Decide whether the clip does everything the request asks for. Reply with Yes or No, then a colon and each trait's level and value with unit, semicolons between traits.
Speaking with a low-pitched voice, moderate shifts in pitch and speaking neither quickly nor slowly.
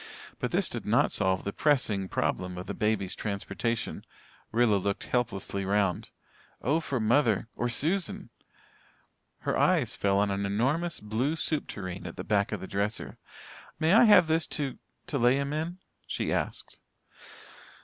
No: low, 110 Hz; wide, 6.6 semitones; average, 160 wpm